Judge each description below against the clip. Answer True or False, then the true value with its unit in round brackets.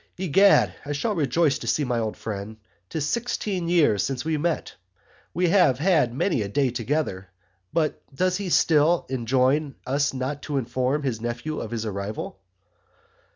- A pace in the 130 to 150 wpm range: False (160 wpm)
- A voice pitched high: False (140 Hz)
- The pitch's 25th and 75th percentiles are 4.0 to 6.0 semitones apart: True (5.6 semitones)